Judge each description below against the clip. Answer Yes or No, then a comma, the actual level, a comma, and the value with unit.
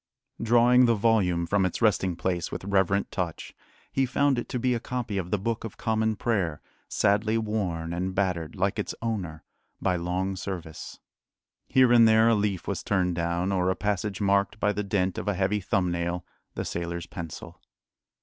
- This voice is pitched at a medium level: No, low, 100 Hz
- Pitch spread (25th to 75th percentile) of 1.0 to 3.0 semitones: No, average, 3.6 semitones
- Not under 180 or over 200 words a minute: Yes, average, 185 wpm